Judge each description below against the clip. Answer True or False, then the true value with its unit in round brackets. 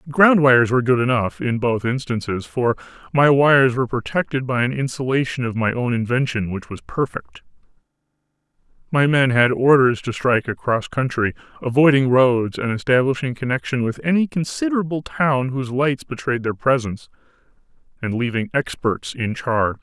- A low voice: True (125 Hz)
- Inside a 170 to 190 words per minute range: False (150 wpm)